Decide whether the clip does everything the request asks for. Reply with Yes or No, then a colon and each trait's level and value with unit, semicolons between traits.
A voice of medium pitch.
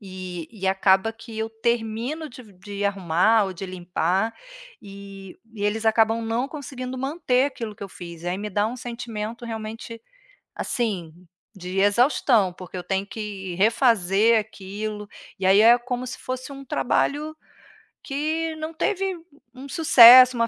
No: high, 220 Hz